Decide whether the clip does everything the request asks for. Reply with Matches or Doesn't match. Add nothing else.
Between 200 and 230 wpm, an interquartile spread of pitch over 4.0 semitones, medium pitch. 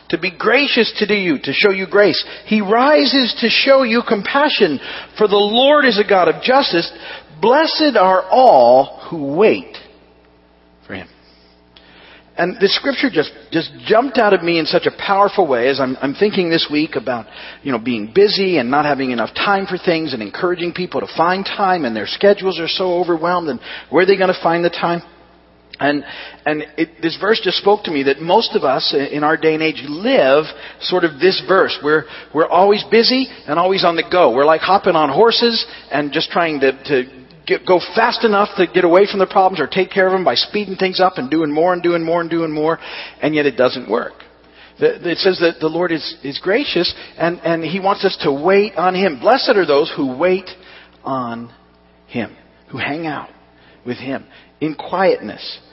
Matches